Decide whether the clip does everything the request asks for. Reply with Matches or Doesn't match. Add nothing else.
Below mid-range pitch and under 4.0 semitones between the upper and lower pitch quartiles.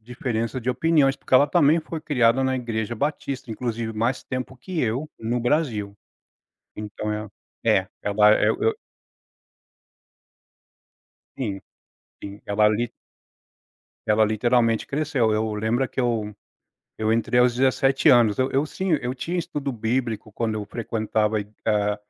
Matches